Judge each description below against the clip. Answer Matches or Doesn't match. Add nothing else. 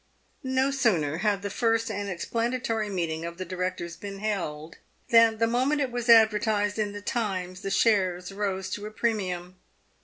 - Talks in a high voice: Matches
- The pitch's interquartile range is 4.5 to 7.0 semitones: Doesn't match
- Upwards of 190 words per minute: Doesn't match